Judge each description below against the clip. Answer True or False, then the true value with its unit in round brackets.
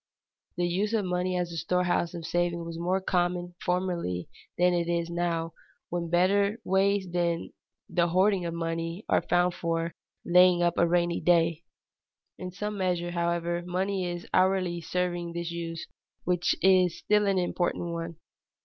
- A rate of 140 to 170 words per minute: True (160 wpm)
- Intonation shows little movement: True (1.3 semitones)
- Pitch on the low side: False (175 Hz)